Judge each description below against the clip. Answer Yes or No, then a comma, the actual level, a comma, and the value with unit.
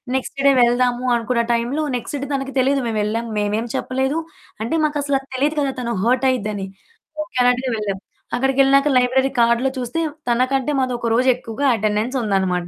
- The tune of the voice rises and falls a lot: No, narrow, 2.6 semitones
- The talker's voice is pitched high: Yes, very high, 250 Hz